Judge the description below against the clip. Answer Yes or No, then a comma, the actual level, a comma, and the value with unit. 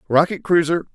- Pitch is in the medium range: Yes, medium, 165 Hz